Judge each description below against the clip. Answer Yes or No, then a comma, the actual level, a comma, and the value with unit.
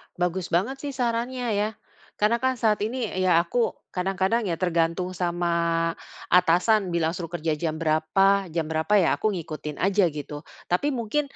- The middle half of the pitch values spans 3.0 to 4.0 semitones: No, average, 4.6 semitones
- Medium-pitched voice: Yes, medium, 180 Hz